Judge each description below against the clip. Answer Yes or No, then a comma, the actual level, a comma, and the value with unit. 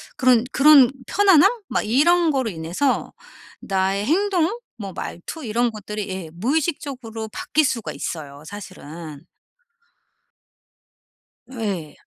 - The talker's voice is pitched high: Yes, high, 230 Hz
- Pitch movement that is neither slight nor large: No, wide, 7.5 semitones